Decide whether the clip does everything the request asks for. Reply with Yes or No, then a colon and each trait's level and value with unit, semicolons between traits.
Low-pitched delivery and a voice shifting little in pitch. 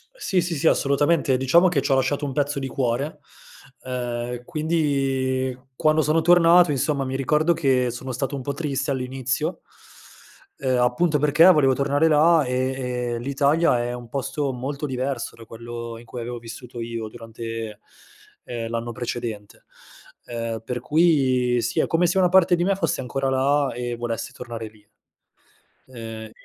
No: low, 130 Hz; average, 3.8 semitones